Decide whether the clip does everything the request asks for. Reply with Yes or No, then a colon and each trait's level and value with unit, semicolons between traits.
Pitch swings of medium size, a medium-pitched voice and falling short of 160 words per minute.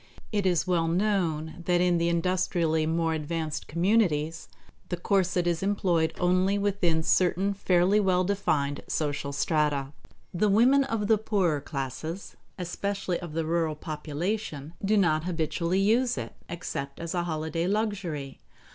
Yes: average, 3.7 semitones; medium, 175 Hz; average, 140 wpm